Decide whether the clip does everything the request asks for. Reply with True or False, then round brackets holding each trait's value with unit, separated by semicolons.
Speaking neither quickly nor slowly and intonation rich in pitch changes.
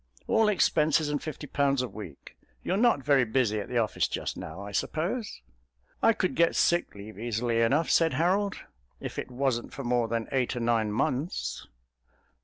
True (180 wpm; 6.0 semitones)